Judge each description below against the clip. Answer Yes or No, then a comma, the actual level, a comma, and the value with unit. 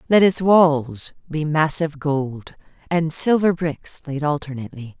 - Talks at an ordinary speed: No, slow, 130 wpm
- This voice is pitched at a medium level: Yes, medium, 155 Hz